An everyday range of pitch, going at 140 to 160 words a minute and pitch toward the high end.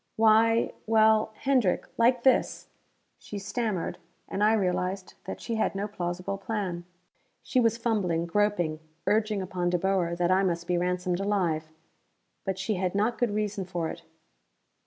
Yes: average, 3.4 semitones; average, 155 wpm; high, 195 Hz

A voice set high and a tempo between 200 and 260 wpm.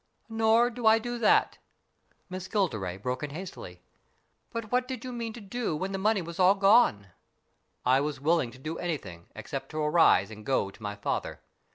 No: medium, 180 Hz; fast, 205 wpm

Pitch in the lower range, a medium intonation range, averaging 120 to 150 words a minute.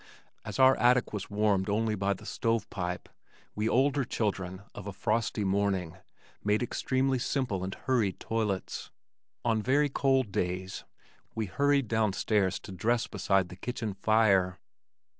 Yes: low, 105 Hz; average, 3.9 semitones; average, 145 wpm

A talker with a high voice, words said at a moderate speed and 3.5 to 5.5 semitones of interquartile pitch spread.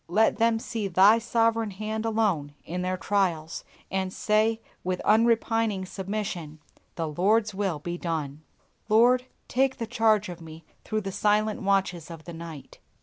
Yes: high, 200 Hz; average, 150 wpm; average, 4.3 semitones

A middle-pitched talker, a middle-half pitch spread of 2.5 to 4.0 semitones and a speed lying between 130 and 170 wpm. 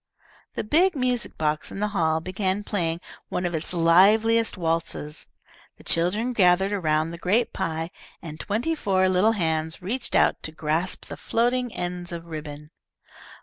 No: medium, 180 Hz; average, 4.5 semitones; average, 155 wpm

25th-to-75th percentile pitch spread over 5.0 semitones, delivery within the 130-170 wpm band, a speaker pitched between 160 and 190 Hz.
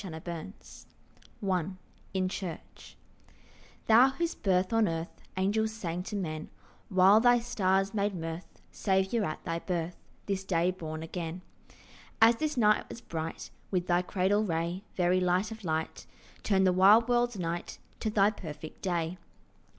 No: average, 3.7 semitones; average, 150 wpm; medium, 185 Hz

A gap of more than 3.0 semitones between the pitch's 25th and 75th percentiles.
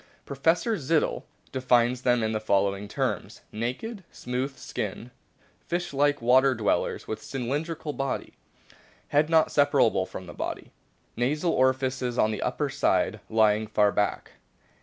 Yes: average, 4.8 semitones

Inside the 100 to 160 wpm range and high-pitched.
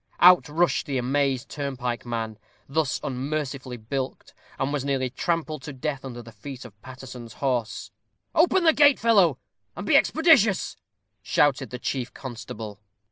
No: average, 145 wpm; low, 135 Hz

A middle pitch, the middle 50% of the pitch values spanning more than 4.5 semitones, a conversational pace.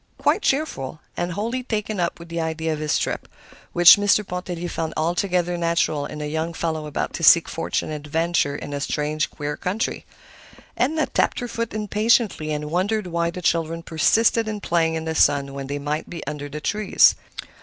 Yes: medium, 170 Hz; average, 4.9 semitones; average, 190 wpm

